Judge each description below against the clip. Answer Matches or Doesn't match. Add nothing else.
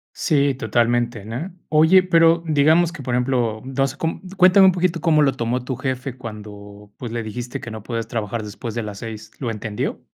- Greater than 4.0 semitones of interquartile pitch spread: Matches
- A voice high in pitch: Doesn't match